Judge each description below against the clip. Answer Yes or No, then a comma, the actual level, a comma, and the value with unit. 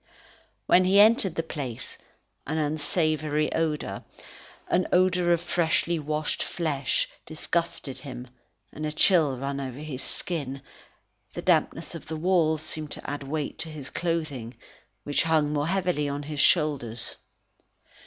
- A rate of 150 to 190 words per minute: No, average, 140 wpm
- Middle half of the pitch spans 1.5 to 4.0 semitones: Yes, average, 2.9 semitones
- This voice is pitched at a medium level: Yes, medium, 155 Hz